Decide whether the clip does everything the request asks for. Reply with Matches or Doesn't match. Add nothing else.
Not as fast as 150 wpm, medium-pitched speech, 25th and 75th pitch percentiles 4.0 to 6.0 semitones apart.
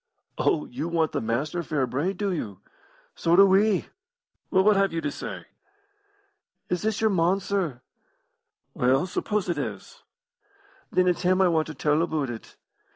Doesn't match